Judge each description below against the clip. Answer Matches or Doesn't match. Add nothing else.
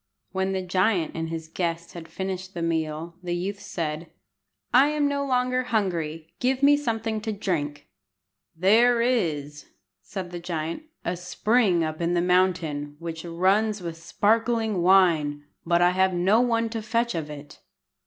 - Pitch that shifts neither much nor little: Matches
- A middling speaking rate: Matches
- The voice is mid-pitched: Matches